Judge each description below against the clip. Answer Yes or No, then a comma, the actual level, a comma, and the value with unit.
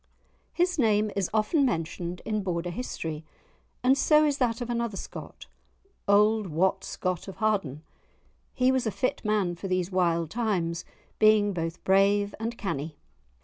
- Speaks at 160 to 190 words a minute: No, average, 150 wpm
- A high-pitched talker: Yes, high, 205 Hz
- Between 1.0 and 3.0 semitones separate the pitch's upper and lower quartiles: No, average, 4.5 semitones